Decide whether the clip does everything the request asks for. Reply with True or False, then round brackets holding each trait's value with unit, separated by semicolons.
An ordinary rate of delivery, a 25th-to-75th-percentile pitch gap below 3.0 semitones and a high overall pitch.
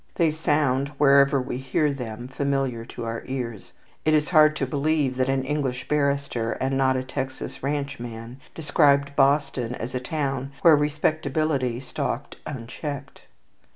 False (150 wpm; 2.5 semitones; 135 Hz)